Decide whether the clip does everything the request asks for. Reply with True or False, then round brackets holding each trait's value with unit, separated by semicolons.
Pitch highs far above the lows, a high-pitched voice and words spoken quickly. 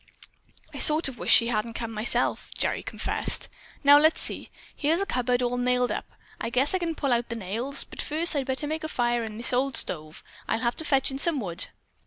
False (3.9 semitones; 250 Hz; 225 wpm)